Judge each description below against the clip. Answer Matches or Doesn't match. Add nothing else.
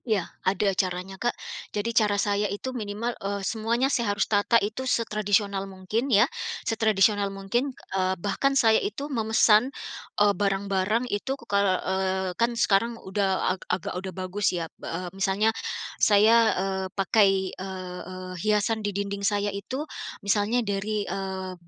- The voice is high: Matches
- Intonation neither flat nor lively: Doesn't match